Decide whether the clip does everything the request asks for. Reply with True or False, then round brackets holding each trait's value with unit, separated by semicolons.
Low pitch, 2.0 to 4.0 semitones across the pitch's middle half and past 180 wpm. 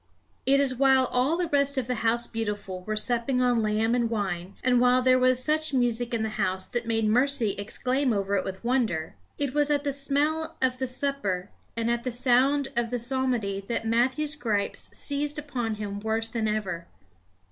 False (245 Hz; 3.7 semitones; 195 wpm)